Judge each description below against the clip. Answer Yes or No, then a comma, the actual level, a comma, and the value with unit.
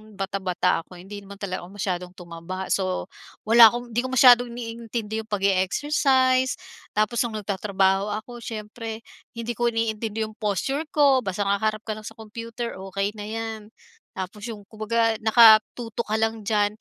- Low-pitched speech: No, high, 220 Hz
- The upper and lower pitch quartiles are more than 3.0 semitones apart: No, narrow, 2.6 semitones